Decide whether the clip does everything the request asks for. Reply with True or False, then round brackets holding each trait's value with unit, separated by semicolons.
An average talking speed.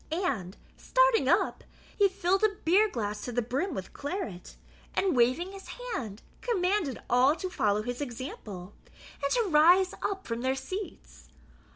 True (155 wpm)